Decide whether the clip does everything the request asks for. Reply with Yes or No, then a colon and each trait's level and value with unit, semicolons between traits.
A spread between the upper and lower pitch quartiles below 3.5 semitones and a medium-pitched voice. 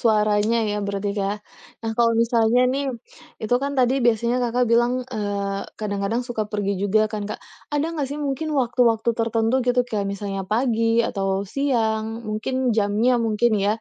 No: average, 2.8 semitones; high, 225 Hz